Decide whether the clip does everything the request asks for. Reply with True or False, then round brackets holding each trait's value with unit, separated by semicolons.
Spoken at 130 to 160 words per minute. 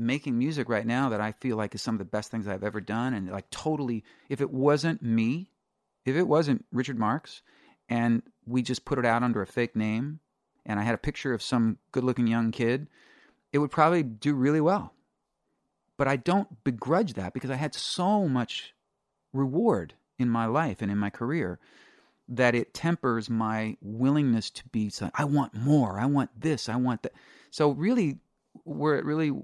False (200 wpm)